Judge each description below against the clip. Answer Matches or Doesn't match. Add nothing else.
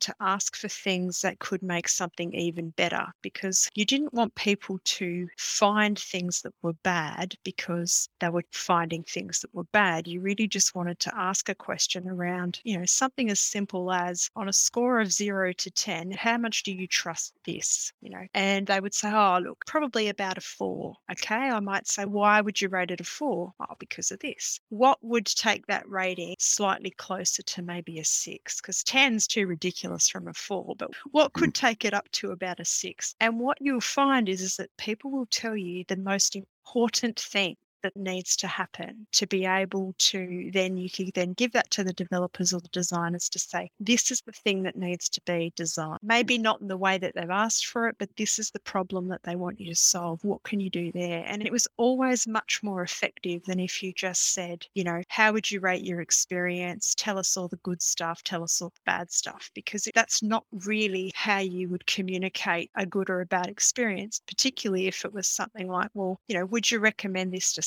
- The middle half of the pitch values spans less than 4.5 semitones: Matches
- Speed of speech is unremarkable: Doesn't match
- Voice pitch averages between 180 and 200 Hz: Matches